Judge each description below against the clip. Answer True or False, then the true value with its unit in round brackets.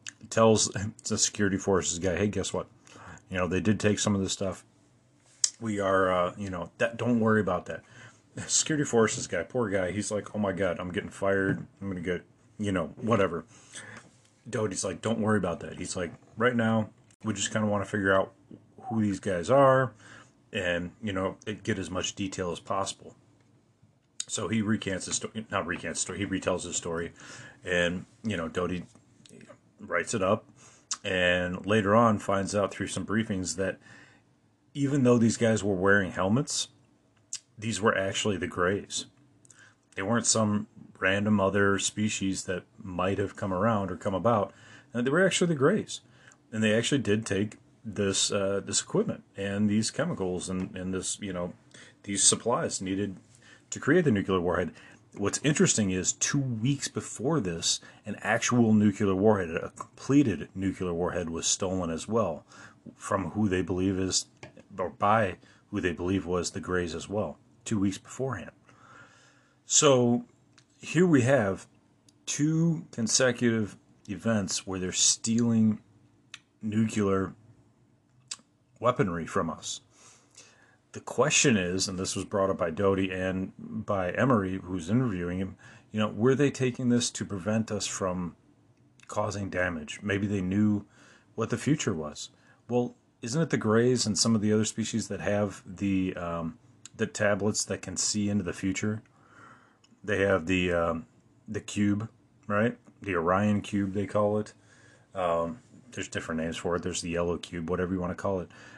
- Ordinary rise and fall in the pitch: True (3.4 semitones)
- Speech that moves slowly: False (165 wpm)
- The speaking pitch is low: True (105 Hz)